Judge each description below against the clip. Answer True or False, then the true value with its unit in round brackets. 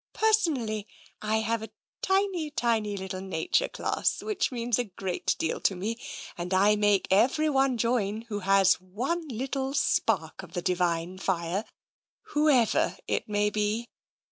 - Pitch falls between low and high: False (215 Hz)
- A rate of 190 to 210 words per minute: False (145 wpm)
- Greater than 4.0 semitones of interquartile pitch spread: True (5.4 semitones)